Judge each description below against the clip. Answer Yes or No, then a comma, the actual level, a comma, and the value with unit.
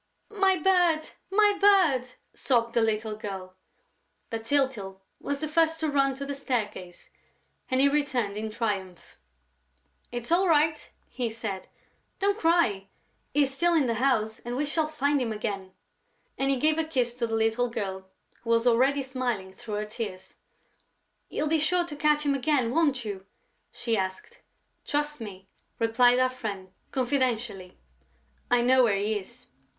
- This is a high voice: Yes, very high, 250 Hz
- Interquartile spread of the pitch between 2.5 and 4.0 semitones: No, average, 5.3 semitones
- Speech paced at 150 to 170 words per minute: Yes, average, 165 wpm